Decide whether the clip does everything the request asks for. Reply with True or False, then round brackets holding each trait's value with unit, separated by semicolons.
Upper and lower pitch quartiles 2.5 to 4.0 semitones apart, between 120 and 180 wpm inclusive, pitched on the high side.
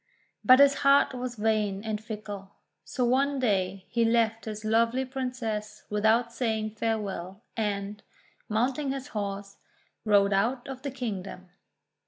True (3.5 semitones; 135 wpm; 220 Hz)